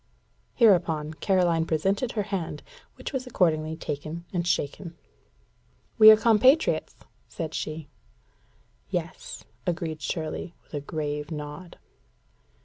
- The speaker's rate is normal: No, slow, 110 wpm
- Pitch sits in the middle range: Yes, medium, 165 Hz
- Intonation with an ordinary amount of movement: Yes, average, 4.1 semitones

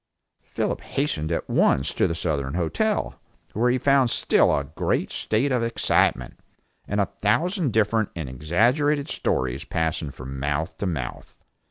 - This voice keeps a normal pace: Yes, average, 150 wpm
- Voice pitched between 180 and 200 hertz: No, very low, 95 Hz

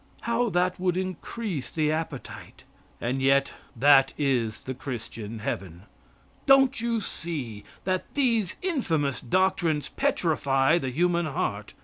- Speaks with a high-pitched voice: No, medium, 155 Hz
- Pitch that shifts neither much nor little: No, wide, 6.1 semitones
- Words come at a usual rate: No, slow, 120 wpm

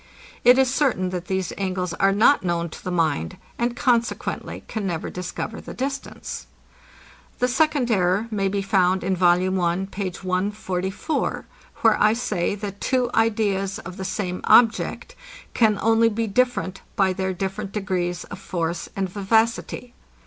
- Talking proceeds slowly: No, average, 155 wpm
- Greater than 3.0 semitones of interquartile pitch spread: Yes, average, 3.7 semitones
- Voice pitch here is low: No, high, 195 Hz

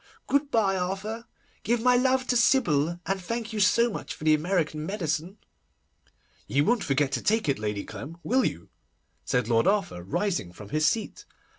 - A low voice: No, medium, 185 Hz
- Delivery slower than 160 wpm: No, average, 175 wpm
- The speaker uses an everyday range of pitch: No, wide, 7.5 semitones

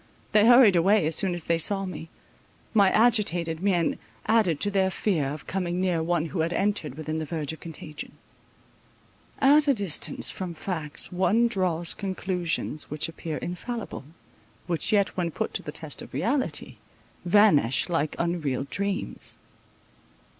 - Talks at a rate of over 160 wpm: No, average, 155 wpm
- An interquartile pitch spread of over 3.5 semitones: Yes, average, 3.9 semitones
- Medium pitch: Yes, medium, 175 Hz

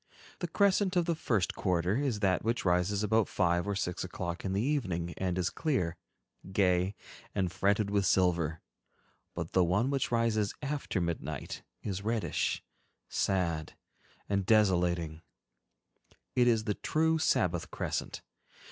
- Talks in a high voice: No, very low, 95 Hz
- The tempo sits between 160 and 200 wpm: No, average, 140 wpm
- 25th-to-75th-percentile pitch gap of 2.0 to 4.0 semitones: No, average, 4.5 semitones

